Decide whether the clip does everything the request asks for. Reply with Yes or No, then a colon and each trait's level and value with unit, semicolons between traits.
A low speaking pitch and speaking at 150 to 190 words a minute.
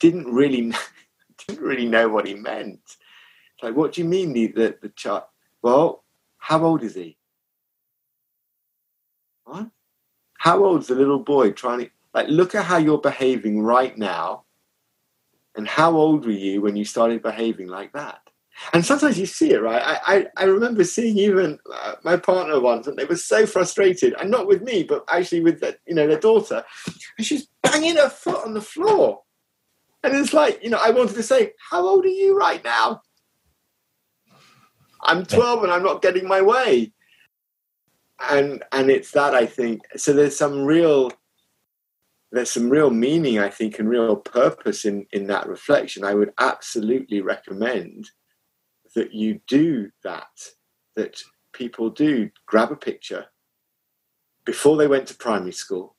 No: medium, 165 Hz; average, 170 wpm